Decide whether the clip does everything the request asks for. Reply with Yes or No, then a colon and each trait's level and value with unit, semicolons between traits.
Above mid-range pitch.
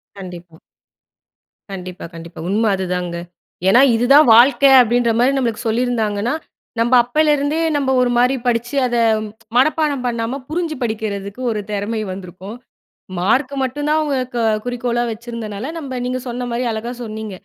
Yes: high, 240 Hz